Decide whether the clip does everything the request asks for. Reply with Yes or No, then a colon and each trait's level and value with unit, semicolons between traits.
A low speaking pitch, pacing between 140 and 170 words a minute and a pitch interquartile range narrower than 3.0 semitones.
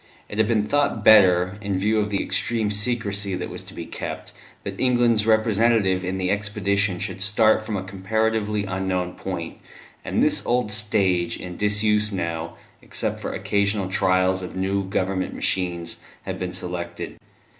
Yes: low, 100 Hz; average, 160 wpm; narrow, 2.4 semitones